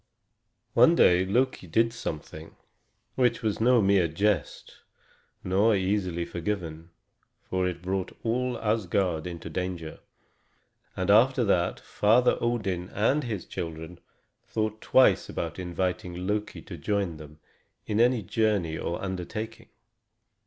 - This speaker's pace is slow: Yes, slow, 120 wpm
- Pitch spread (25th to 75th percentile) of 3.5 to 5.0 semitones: Yes, average, 4.2 semitones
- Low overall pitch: Yes, very low, 95 Hz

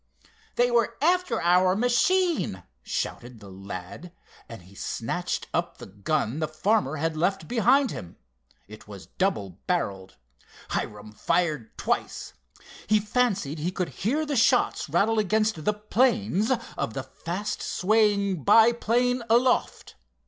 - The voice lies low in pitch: No, high, 190 Hz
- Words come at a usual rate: No, slow, 130 wpm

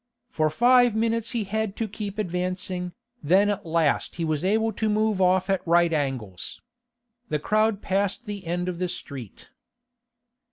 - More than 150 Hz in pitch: Yes, high, 190 Hz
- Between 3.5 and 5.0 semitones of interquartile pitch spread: Yes, average, 4.2 semitones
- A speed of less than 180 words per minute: Yes, average, 160 wpm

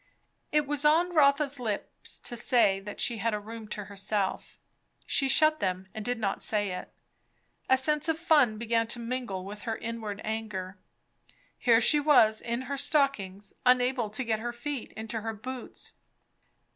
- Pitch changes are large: No, average, 4.4 semitones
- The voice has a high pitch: Yes, high, 230 Hz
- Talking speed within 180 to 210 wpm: No, average, 170 wpm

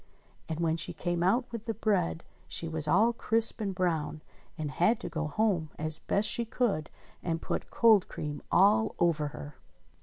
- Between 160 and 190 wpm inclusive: Yes, average, 180 wpm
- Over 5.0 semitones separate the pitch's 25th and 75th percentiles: Yes, wide, 5.6 semitones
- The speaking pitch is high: No, medium, 175 Hz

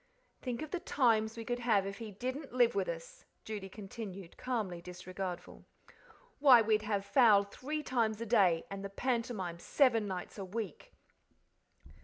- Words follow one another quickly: No, average, 160 wpm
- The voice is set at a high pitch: Yes, high, 215 Hz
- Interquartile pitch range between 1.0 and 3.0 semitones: No, average, 3.9 semitones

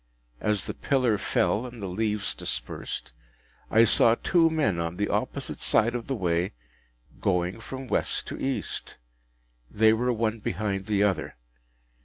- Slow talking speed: No, average, 150 wpm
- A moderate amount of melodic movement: Yes, average, 3.7 semitones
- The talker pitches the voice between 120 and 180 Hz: No, low, 110 Hz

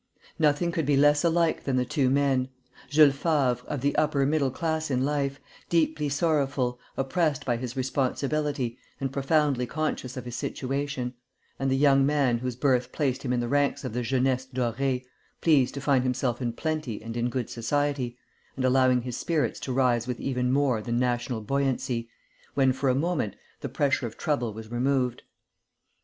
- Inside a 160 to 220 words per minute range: Yes, average, 175 wpm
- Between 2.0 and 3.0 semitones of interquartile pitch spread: Yes, narrow, 2.5 semitones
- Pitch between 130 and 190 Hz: Yes, low, 135 Hz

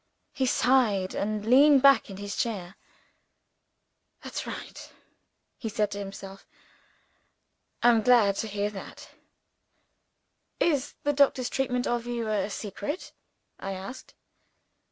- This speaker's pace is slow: Yes, slow, 115 wpm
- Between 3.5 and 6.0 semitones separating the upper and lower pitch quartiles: Yes, average, 4.2 semitones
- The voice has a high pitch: Yes, high, 220 Hz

